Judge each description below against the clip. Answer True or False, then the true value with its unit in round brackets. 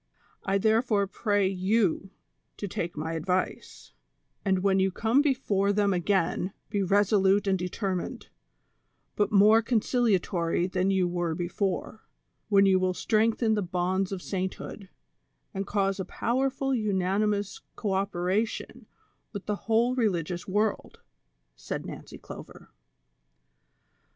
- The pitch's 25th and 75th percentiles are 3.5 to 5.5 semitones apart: False (2.5 semitones)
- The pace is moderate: False (125 wpm)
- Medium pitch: False (195 Hz)